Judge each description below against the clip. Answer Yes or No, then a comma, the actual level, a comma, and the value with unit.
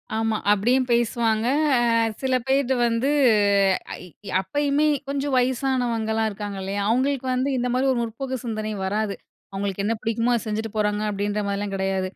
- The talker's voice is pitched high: Yes, high, 225 Hz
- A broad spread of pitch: No, average, 3.8 semitones